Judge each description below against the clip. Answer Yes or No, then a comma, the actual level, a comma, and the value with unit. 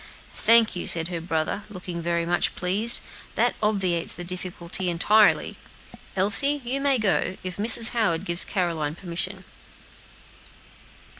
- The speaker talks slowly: Yes, slow, 130 wpm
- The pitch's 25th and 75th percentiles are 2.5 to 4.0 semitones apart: Yes, average, 3.7 semitones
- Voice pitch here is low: No, medium, 185 Hz